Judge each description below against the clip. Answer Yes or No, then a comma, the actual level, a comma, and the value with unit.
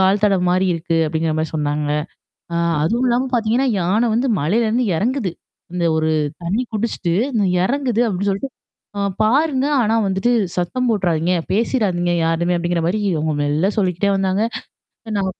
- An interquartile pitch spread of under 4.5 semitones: No, average, 5.0 semitones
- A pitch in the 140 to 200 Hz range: Yes, high, 190 Hz